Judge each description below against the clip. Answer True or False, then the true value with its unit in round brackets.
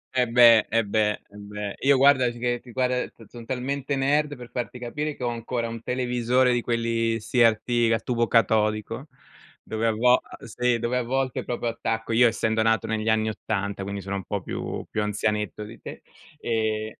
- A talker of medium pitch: False (115 Hz)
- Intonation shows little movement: True (2.2 semitones)